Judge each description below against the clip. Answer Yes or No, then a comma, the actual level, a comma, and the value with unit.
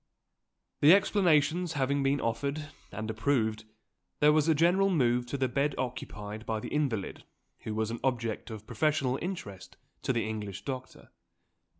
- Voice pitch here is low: Yes, low, 130 Hz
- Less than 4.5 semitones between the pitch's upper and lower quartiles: No, average, 5.3 semitones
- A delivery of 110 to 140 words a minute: No, average, 155 wpm